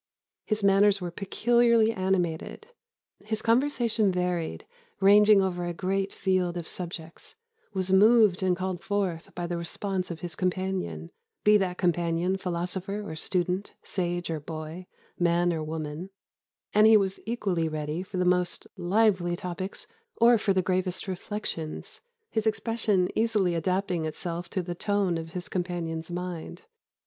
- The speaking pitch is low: No, medium, 185 Hz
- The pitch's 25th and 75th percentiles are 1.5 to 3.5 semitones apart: Yes, narrow, 2.6 semitones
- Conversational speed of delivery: Yes, average, 145 wpm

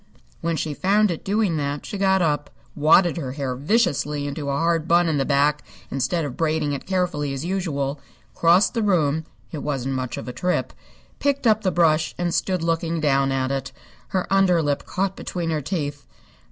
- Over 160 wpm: Yes, average, 195 wpm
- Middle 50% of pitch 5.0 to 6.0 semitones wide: No, average, 4.1 semitones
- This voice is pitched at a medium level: Yes, medium, 160 Hz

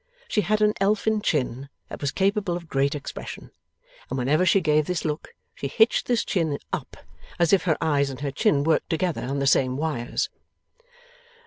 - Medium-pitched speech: Yes, medium, 155 Hz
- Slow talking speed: No, average, 185 wpm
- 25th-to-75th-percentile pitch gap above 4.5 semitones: Yes, average, 5.1 semitones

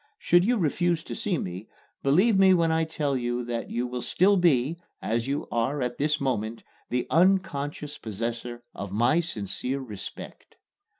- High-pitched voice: No, medium, 140 Hz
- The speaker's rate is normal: Yes, average, 165 wpm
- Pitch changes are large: Yes, wide, 5.9 semitones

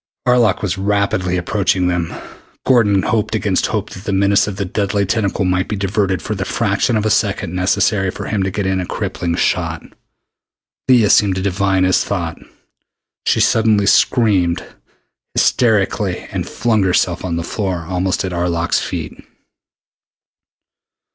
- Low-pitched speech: Yes, very low, 95 Hz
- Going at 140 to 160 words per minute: Yes, average, 155 wpm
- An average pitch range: No, narrow, 2.2 semitones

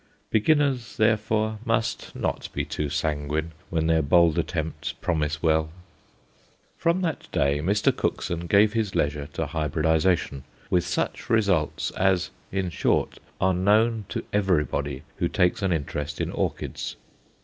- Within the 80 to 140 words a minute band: Yes, slow, 135 wpm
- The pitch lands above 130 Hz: No, very low, 85 Hz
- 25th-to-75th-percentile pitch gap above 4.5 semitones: Yes, wide, 5.6 semitones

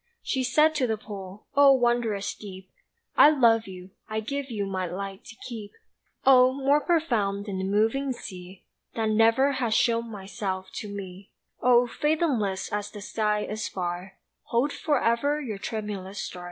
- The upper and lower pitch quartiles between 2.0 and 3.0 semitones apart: No, average, 4.5 semitones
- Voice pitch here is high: Yes, high, 220 Hz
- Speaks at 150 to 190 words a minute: Yes, average, 160 wpm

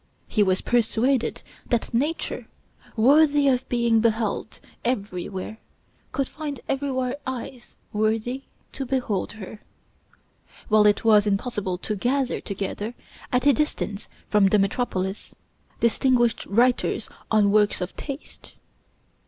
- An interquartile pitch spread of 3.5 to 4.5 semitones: Yes, average, 3.8 semitones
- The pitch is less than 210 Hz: No, high, 230 Hz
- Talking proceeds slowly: Yes, slow, 115 wpm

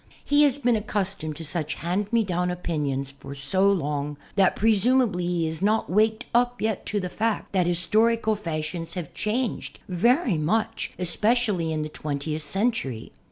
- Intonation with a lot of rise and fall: Yes, wide, 5.7 semitones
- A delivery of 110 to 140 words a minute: No, average, 165 wpm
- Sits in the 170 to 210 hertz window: Yes, medium, 185 Hz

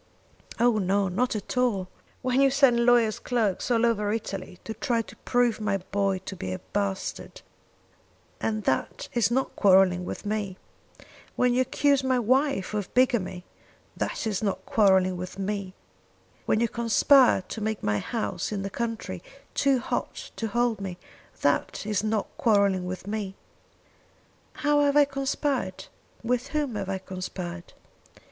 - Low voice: No, high, 215 Hz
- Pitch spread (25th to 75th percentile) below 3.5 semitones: No, average, 4.2 semitones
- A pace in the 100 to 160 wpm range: Yes, average, 155 wpm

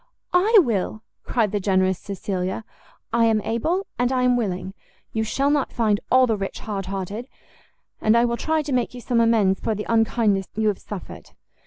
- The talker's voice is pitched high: Yes, high, 220 Hz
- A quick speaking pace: No, average, 185 wpm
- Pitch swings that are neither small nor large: Yes, average, 3.8 semitones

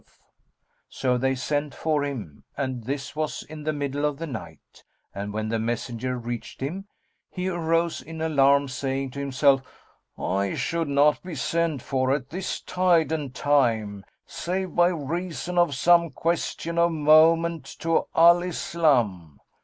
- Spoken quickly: No, average, 155 wpm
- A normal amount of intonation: Yes, average, 4.3 semitones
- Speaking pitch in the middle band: Yes, medium, 145 Hz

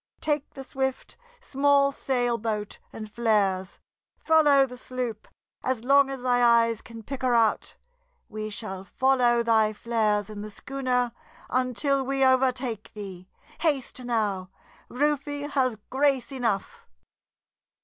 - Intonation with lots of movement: No, average, 3.7 semitones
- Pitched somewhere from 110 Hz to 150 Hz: No, high, 245 Hz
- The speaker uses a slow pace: Yes, slow, 125 wpm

